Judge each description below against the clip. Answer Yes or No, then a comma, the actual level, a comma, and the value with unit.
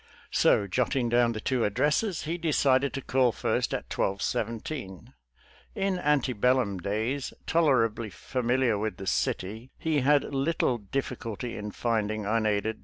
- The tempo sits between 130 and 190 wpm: Yes, average, 150 wpm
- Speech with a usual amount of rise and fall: Yes, average, 4.2 semitones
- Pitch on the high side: No, low, 120 Hz